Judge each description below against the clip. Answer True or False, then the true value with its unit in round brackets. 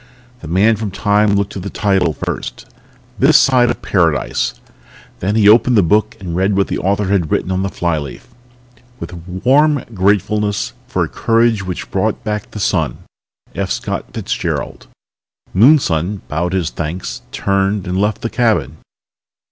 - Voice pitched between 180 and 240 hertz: False (100 Hz)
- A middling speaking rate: True (155 wpm)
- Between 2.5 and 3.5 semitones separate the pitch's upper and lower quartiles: True (2.9 semitones)